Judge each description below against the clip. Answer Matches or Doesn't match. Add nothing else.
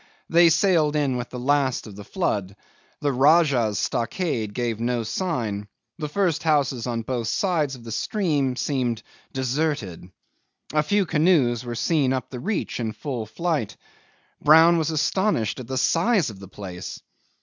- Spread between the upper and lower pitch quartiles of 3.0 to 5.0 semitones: Doesn't match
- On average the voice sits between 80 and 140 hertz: Matches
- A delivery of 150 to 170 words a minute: Matches